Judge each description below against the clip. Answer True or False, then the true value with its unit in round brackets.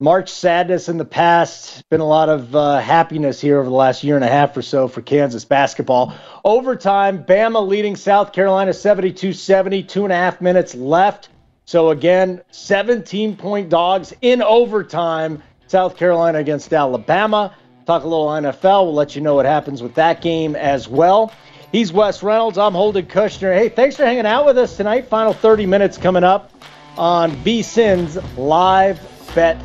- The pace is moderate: True (170 wpm)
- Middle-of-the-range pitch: True (180 Hz)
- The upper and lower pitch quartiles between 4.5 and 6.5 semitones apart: True (4.9 semitones)